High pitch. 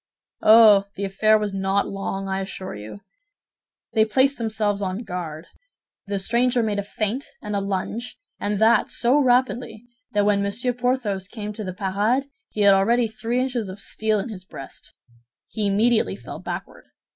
Yes: high, 210 Hz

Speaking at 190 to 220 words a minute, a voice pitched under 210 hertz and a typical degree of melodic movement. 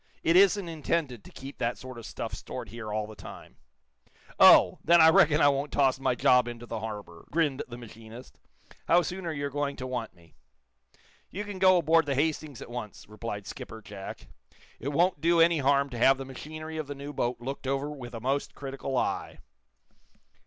Yes: average, 200 wpm; low, 135 Hz; average, 4.7 semitones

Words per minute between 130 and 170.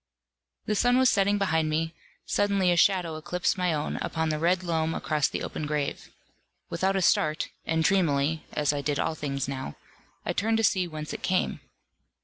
No: average, 185 wpm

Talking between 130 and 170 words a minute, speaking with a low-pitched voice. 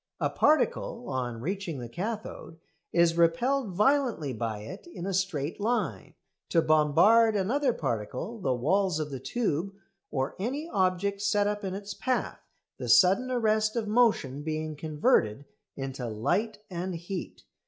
No: average, 145 wpm; medium, 185 Hz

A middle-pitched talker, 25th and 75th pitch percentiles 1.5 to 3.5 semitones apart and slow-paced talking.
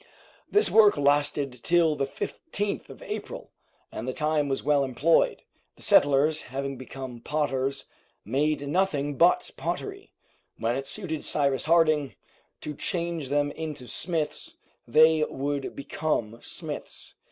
Yes: medium, 145 Hz; average, 2.7 semitones; slow, 130 wpm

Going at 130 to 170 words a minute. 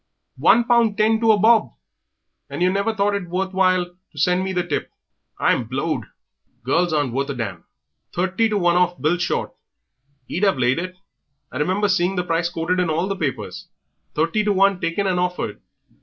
No: average, 190 wpm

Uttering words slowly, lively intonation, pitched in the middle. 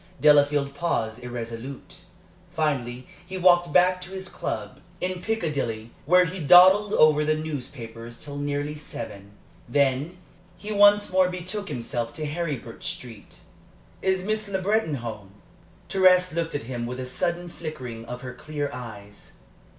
No: average, 145 wpm; wide, 6.7 semitones; medium, 150 Hz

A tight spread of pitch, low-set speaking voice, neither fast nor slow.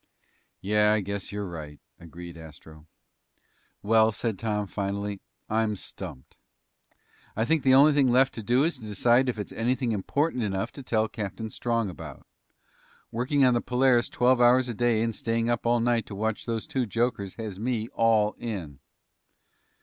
No: average, 3.2 semitones; low, 110 Hz; average, 170 wpm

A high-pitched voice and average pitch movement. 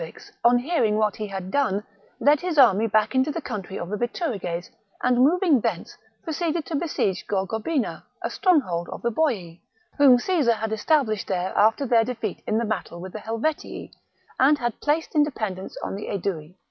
No: high, 230 Hz; wide, 6.6 semitones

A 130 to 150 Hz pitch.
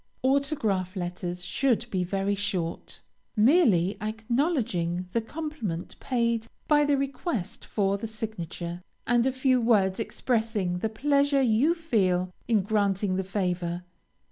No: high, 215 Hz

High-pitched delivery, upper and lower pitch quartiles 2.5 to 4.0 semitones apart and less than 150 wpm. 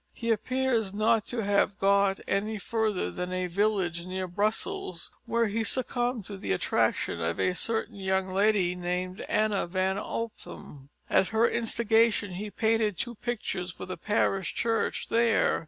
No: high, 205 Hz; average, 3.5 semitones; average, 155 wpm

